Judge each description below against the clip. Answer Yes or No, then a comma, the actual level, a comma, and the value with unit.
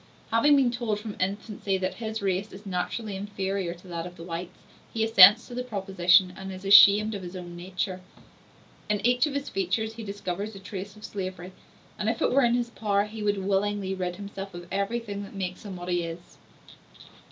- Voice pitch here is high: Yes, high, 200 Hz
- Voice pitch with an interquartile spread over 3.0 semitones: No, average, 2.7 semitones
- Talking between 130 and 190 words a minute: No, fast, 205 wpm